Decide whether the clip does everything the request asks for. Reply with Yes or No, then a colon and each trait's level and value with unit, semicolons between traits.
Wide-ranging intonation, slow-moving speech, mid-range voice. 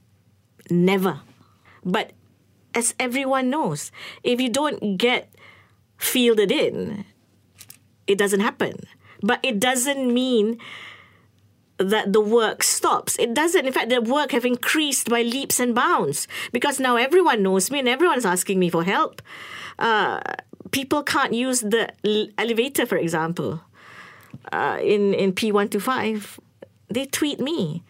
No: wide, 7.5 semitones; slow, 130 wpm; high, 220 Hz